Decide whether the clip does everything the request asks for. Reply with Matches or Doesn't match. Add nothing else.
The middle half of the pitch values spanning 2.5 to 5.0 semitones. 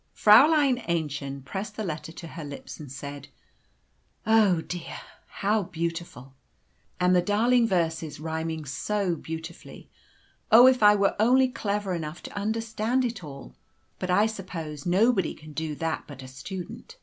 Doesn't match